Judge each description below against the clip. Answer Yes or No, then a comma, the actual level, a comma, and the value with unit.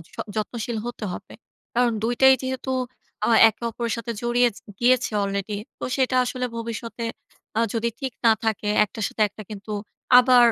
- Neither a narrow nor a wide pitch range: No, narrow, 2.0 semitones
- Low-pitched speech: No, high, 235 Hz